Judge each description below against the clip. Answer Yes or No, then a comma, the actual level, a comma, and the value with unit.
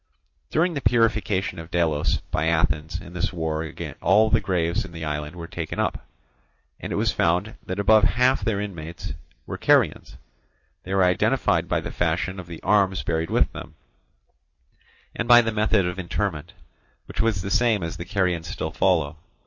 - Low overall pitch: Yes, very low, 90 Hz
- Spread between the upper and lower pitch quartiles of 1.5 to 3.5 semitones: No, average, 4.1 semitones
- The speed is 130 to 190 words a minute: Yes, average, 175 wpm